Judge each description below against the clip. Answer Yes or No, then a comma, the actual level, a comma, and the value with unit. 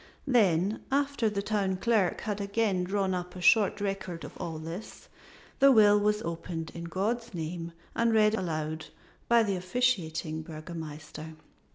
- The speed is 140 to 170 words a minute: Yes, average, 150 wpm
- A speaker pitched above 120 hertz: Yes, high, 190 Hz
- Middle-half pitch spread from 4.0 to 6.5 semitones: Yes, average, 4.4 semitones